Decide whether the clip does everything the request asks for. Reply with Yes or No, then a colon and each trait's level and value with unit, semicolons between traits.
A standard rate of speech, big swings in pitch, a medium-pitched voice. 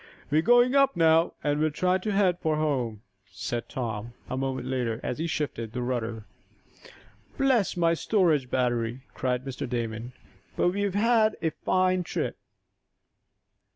Yes: average, 155 wpm; wide, 7.0 semitones; medium, 150 Hz